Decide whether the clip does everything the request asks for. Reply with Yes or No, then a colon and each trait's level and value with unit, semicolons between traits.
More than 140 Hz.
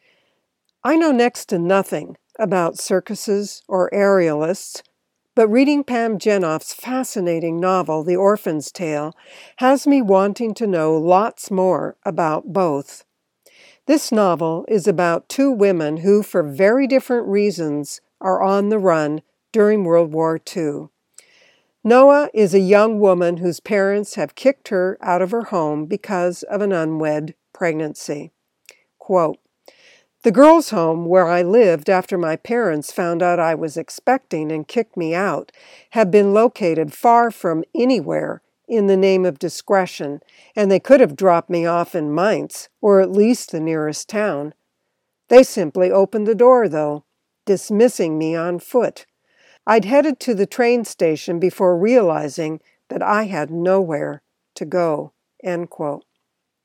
Yes: high, 190 Hz